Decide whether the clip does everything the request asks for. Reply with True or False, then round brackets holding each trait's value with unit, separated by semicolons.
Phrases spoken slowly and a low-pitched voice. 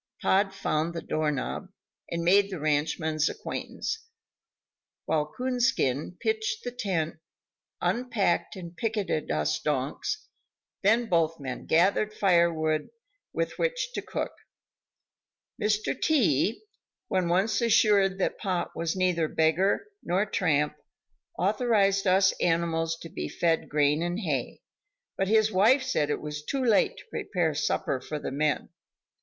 False (130 wpm; 180 Hz)